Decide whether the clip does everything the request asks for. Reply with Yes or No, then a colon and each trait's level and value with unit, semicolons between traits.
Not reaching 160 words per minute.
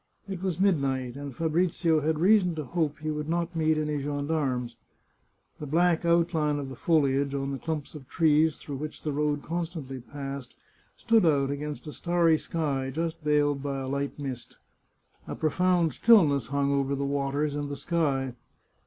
No: average, 170 wpm